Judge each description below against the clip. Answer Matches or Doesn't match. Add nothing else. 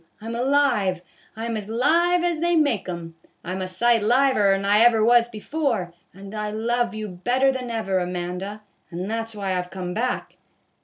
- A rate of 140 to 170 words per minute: Doesn't match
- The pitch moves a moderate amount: Matches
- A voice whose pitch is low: Doesn't match